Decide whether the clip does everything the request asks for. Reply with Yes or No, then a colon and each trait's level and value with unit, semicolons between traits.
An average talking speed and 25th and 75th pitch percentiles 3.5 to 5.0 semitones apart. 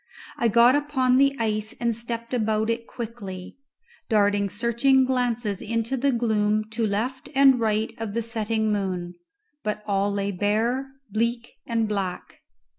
No: average, 145 wpm; narrow, 2.4 semitones